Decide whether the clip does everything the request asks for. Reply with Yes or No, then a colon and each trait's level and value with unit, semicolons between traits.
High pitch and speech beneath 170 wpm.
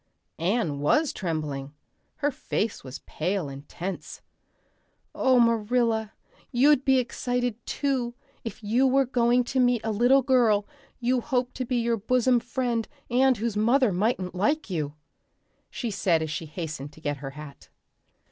Yes: high, 230 Hz; average, 150 wpm